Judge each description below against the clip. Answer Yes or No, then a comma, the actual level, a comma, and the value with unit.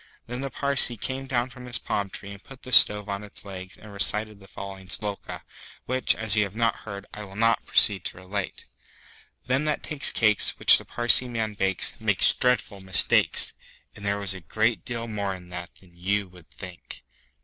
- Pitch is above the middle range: No, low, 105 Hz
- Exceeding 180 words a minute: Yes, average, 200 wpm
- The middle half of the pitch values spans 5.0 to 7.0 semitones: No, average, 3.6 semitones